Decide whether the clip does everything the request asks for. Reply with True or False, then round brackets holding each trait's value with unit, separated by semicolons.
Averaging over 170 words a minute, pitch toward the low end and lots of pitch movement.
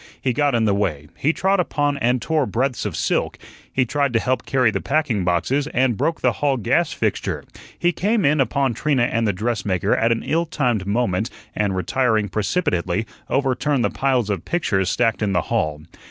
True (195 wpm; 120 Hz; 5.7 semitones)